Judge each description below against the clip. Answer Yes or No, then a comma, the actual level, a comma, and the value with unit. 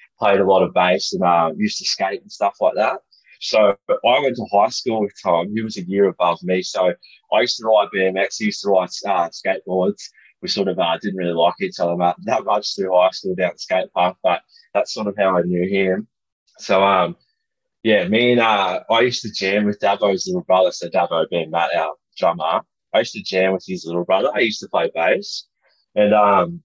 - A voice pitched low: Yes, very low, 95 Hz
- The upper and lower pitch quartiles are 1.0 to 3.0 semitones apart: No, average, 3.6 semitones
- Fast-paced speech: Yes, fast, 230 wpm